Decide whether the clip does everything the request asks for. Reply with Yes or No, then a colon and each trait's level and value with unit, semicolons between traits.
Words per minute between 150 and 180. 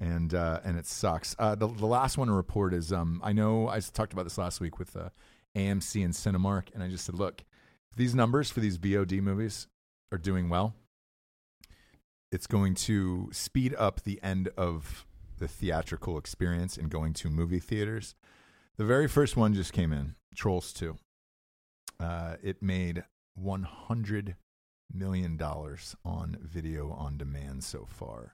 Yes: average, 165 wpm